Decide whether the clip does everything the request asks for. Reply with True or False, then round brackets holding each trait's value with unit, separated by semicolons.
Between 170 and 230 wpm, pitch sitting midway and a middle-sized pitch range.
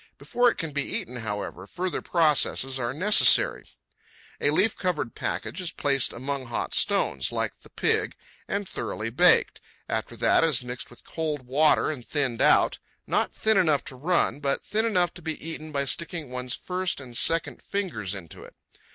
False (175 wpm; 145 Hz; 5.8 semitones)